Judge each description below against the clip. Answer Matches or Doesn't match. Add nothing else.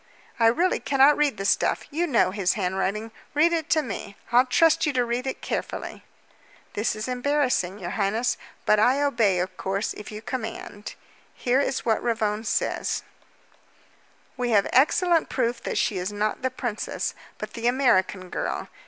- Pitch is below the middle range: Doesn't match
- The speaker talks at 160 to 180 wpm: Matches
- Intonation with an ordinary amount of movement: Matches